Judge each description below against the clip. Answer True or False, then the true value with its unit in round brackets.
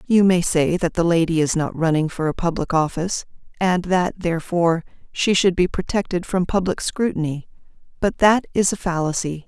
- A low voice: False (175 Hz)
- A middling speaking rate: True (175 wpm)